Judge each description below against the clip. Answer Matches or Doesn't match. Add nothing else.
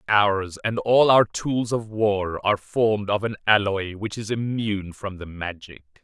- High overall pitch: Doesn't match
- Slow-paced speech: Doesn't match